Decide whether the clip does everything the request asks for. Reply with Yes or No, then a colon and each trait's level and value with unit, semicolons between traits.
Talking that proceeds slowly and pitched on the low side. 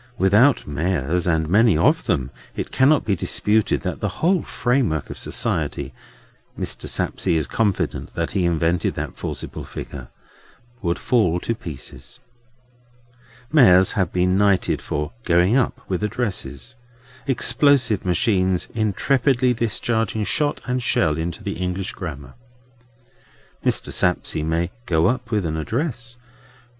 Yes: slow, 125 wpm; very low, 95 Hz